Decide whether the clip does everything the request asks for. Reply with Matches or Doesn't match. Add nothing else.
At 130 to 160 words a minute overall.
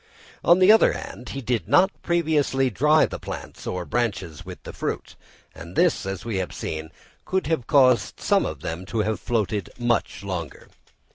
Doesn't match